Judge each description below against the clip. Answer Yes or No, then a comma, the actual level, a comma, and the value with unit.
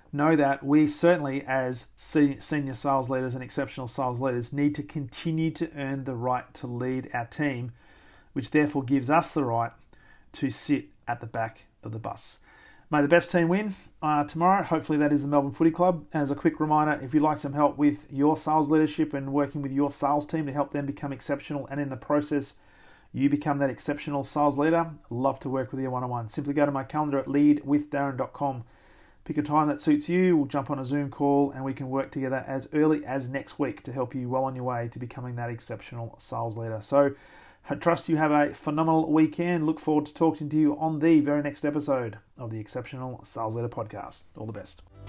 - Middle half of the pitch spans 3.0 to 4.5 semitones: No, narrow, 2.6 semitones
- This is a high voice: No, medium, 140 Hz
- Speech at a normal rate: No, fast, 215 wpm